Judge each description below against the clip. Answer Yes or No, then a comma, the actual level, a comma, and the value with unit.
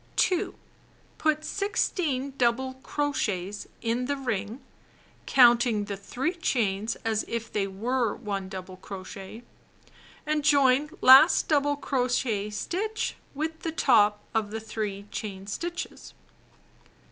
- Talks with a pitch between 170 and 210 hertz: No, high, 240 Hz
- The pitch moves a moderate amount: No, wide, 5.7 semitones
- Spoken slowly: Yes, slow, 125 wpm